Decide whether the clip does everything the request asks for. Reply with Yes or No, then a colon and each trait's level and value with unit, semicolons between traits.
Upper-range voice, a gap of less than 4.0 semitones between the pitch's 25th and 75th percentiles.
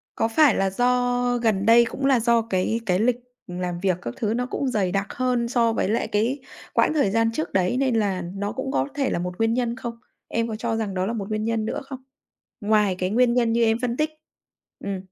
Yes: high, 225 Hz; average, 3.6 semitones